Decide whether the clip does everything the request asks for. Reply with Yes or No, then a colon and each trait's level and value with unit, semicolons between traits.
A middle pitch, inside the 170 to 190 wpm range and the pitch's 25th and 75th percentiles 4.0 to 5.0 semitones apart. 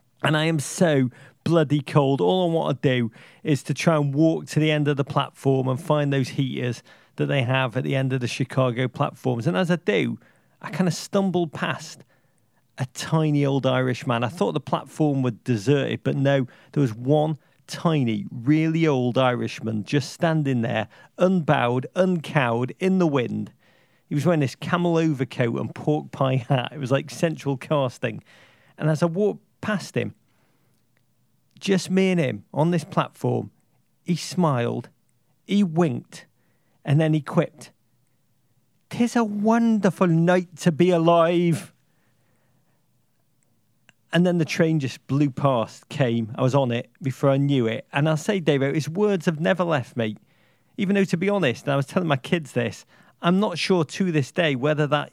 Yes: medium, 145 Hz; average, 175 wpm; average, 4.7 semitones